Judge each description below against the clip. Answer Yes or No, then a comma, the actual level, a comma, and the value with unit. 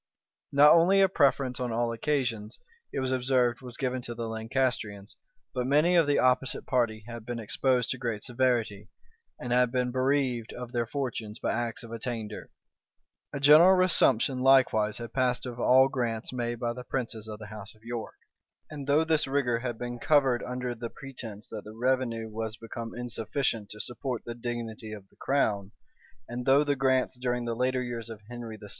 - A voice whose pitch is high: No, low, 120 Hz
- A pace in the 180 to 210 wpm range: Yes, average, 190 wpm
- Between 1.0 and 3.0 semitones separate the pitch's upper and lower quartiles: Yes, narrow, 2.5 semitones